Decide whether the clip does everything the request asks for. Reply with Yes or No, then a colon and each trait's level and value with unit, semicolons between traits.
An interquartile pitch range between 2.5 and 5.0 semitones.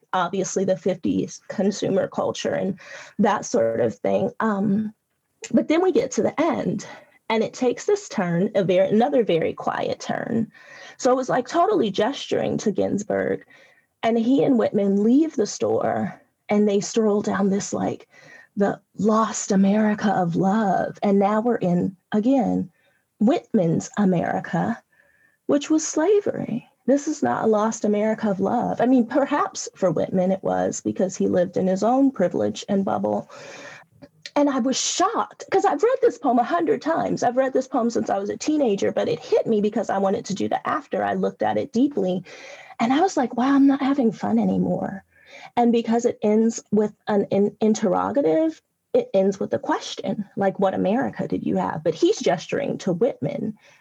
No: wide, 5.4 semitones